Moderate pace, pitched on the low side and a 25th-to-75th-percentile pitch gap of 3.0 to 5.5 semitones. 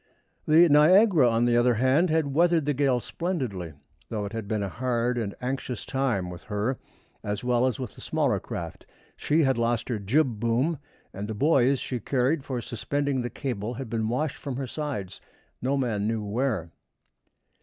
Yes: average, 185 wpm; low, 125 Hz; average, 4.1 semitones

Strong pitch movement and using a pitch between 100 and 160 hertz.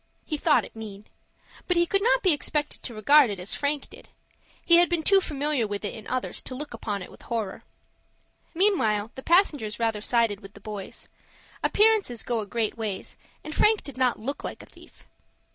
No: wide, 6.8 semitones; very high, 250 Hz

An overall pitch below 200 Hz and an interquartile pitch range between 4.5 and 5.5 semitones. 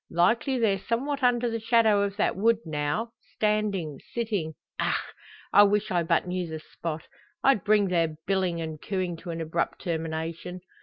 Yes: high, 190 Hz; average, 4.8 semitones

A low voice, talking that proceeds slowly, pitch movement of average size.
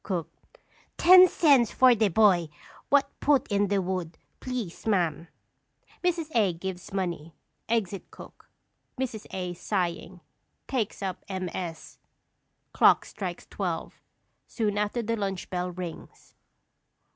No: high, 195 Hz; slow, 120 wpm; average, 4.5 semitones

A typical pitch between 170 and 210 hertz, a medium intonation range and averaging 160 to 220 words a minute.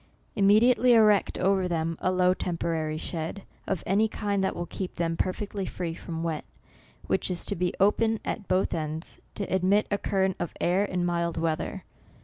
Yes: medium, 185 Hz; average, 3.0 semitones; average, 180 wpm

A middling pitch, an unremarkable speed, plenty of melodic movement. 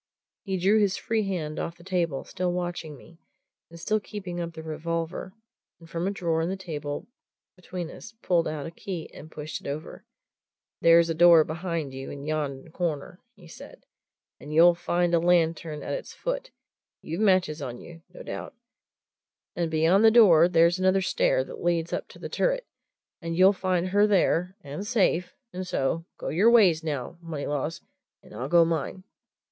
No: medium, 170 Hz; average, 180 wpm; average, 2.7 semitones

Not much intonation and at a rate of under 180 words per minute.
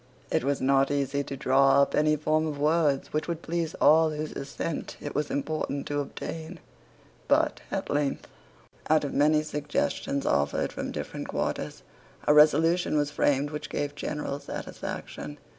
Yes: narrow, 1.7 semitones; average, 160 wpm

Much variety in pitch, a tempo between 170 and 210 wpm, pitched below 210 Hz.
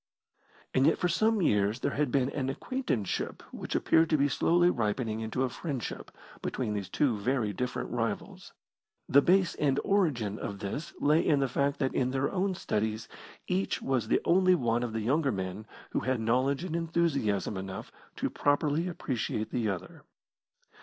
Yes: wide, 6.4 semitones; average, 175 wpm; low, 135 Hz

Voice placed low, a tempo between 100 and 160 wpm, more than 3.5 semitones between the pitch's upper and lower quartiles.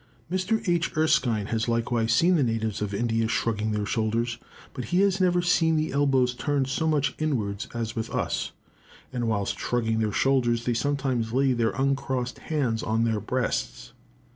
No: low, 120 Hz; average, 170 wpm; average, 4.2 semitones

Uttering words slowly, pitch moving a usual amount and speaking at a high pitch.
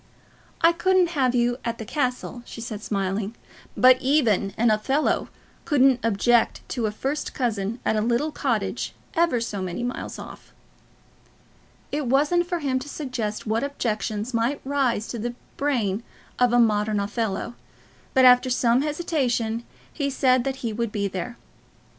No: average, 155 wpm; average, 3.8 semitones; high, 240 Hz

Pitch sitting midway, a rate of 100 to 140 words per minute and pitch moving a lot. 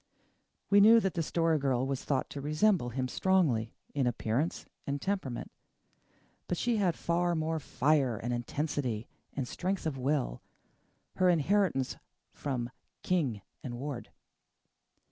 Yes: medium, 145 Hz; slow, 135 wpm; wide, 5.7 semitones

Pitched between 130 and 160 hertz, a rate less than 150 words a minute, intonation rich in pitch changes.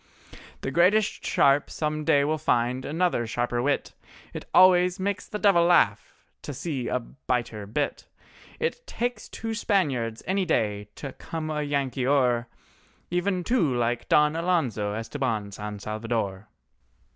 Yes: medium, 140 Hz; average, 140 wpm; wide, 6.9 semitones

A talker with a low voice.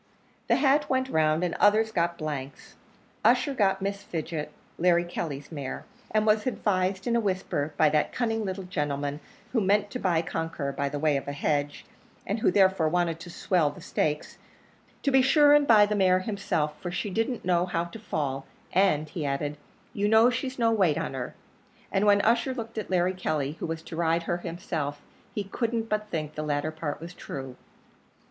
No: medium, 180 Hz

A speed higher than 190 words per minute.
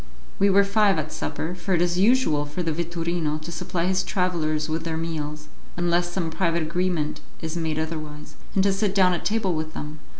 Yes: average, 200 wpm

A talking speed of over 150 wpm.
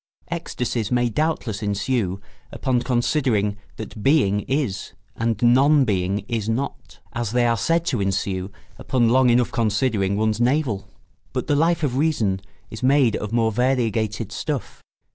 No: average, 145 wpm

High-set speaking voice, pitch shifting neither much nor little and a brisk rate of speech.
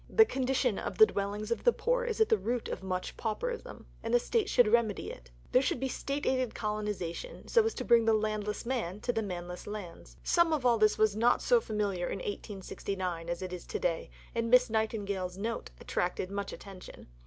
Yes: high, 215 Hz; average, 4.4 semitones; fast, 210 wpm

